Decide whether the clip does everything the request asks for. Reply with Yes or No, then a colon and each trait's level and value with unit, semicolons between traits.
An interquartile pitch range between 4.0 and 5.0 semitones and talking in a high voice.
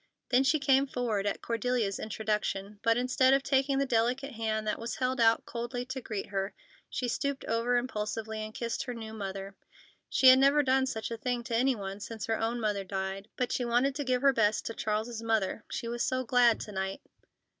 No: average, 3.1 semitones; high, 235 Hz